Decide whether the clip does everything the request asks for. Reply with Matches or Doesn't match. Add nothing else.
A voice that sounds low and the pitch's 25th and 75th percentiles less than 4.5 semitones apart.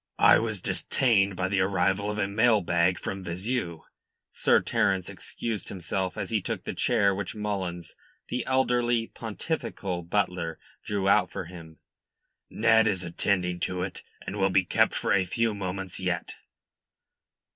Matches